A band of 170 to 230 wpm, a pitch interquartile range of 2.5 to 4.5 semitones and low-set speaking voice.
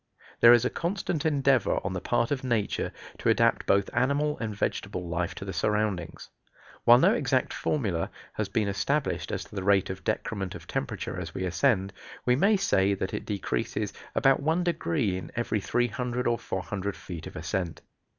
No: average, 180 wpm; wide, 5.5 semitones; low, 105 Hz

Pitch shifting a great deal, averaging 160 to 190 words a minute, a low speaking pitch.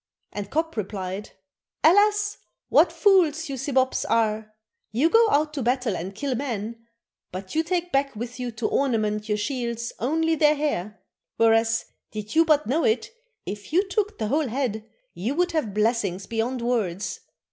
No: wide, 6.2 semitones; average, 165 wpm; high, 245 Hz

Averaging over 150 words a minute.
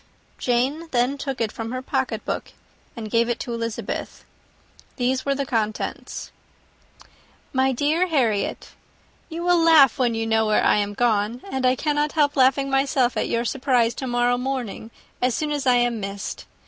Yes: average, 185 wpm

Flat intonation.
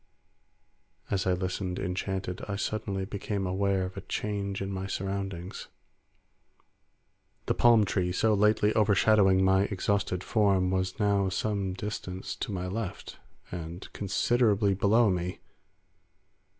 Yes: narrow, 1.8 semitones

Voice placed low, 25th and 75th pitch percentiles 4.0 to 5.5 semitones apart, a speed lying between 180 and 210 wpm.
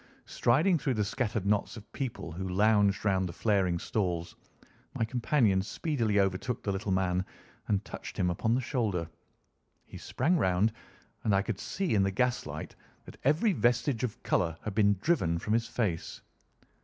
No: low, 105 Hz; average, 4.3 semitones; average, 170 wpm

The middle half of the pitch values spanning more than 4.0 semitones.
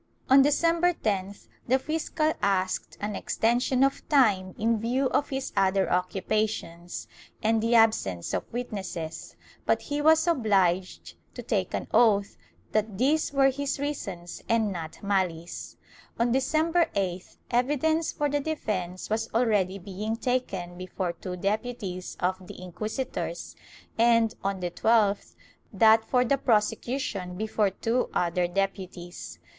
Yes: wide, 5.6 semitones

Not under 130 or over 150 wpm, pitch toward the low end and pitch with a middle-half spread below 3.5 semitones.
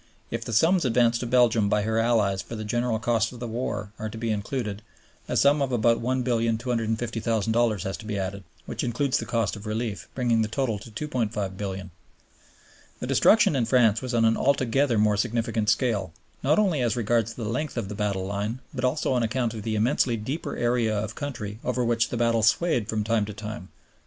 No: average, 200 wpm; low, 115 Hz; narrow, 2.5 semitones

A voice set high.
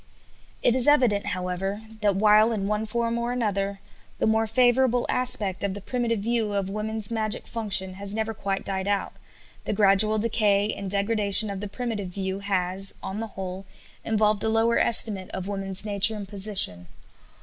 Yes: high, 205 Hz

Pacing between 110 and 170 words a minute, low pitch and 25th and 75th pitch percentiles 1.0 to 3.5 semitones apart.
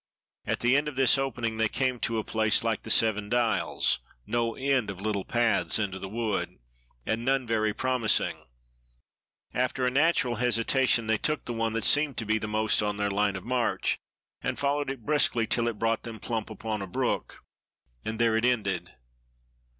No: average, 185 wpm; low, 115 Hz; average, 2.7 semitones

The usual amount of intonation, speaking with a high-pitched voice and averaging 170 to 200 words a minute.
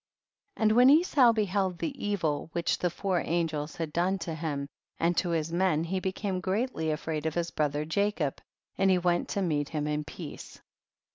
No: average, 3.7 semitones; medium, 170 Hz; average, 190 wpm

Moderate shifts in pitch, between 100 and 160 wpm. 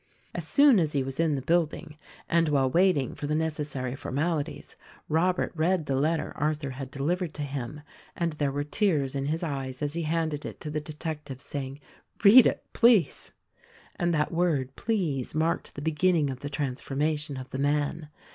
No: average, 3.1 semitones; average, 185 wpm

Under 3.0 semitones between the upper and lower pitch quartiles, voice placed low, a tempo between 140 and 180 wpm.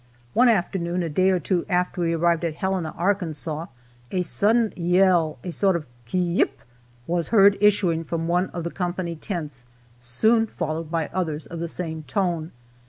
No: narrow, 2.6 semitones; medium, 175 Hz; average, 170 wpm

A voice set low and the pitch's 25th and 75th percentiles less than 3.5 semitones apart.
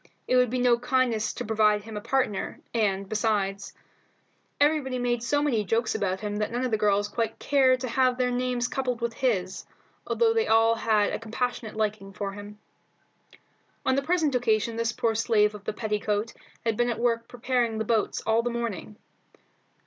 No: high, 230 Hz; average, 2.9 semitones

